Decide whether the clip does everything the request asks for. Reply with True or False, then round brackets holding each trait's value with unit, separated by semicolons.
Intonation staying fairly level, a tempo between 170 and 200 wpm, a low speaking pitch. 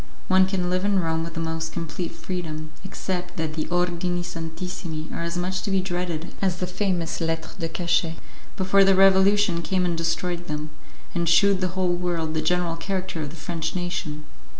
False (2.2 semitones; 190 wpm; 175 Hz)